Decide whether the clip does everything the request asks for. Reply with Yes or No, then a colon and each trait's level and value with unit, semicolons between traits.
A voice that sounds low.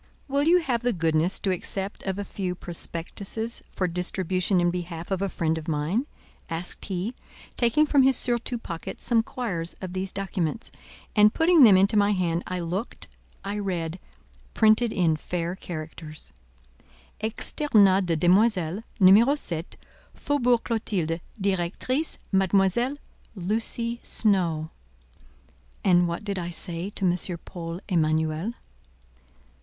No: high, 190 Hz